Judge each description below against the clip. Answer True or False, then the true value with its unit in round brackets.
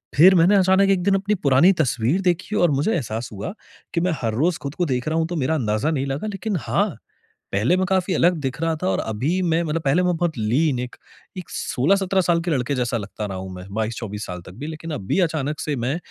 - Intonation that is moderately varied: False (6.6 semitones)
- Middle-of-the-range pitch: True (155 Hz)